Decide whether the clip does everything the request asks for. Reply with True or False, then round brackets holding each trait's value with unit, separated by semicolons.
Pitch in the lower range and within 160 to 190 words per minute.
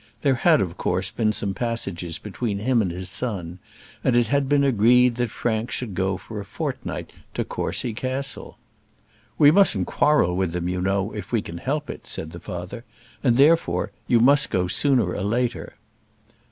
True (110 Hz; 180 wpm)